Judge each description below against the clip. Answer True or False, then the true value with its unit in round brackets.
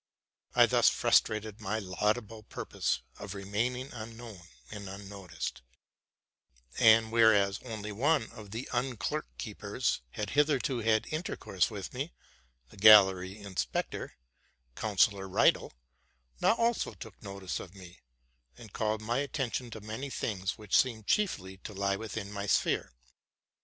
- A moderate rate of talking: False (125 wpm)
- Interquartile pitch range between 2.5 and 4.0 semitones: True (2.9 semitones)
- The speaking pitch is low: True (110 Hz)